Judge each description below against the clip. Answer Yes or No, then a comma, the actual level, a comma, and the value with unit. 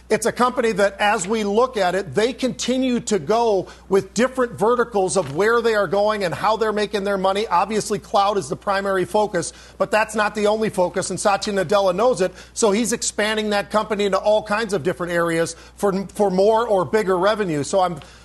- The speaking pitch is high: Yes, high, 205 Hz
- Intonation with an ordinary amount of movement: No, narrow, 2.1 semitones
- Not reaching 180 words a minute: No, fast, 205 wpm